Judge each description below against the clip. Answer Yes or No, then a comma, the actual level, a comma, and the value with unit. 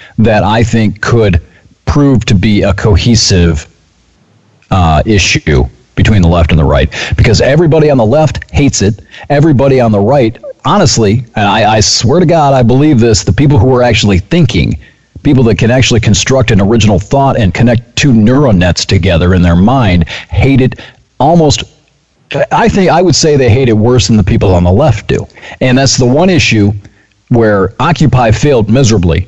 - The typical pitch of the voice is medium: No, low, 110 Hz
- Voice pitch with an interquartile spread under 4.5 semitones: No, average, 4.8 semitones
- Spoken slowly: No, average, 180 wpm